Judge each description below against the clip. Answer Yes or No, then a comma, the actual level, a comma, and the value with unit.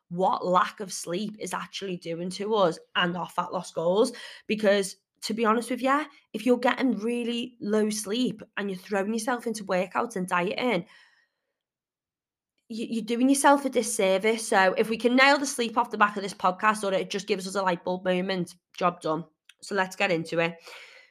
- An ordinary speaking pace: Yes, average, 195 wpm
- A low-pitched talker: No, high, 215 Hz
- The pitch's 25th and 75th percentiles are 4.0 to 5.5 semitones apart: Yes, average, 4.5 semitones